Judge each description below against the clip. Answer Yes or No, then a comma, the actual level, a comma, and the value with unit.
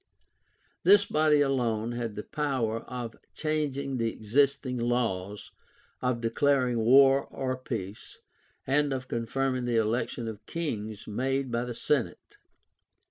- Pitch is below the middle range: Yes, low, 125 Hz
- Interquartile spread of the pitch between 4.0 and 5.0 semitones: No, average, 3.3 semitones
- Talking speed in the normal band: No, slow, 125 wpm